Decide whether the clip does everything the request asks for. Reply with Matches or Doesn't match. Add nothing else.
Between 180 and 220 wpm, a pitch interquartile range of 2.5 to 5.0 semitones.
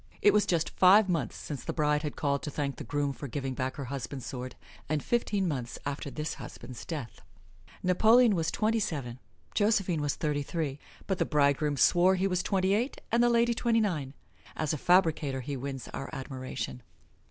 Doesn't match